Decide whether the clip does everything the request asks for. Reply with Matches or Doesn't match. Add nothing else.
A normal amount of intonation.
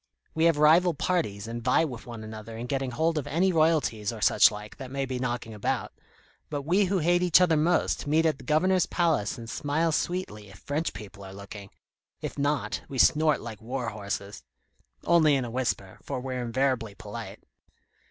Doesn't match